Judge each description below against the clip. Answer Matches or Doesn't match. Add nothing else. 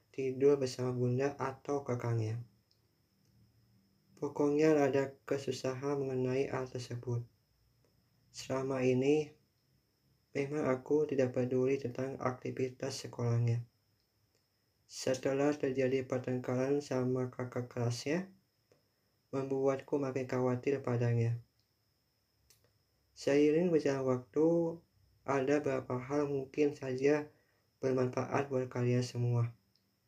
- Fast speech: Doesn't match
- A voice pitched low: Matches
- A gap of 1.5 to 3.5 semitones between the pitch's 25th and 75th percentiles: Matches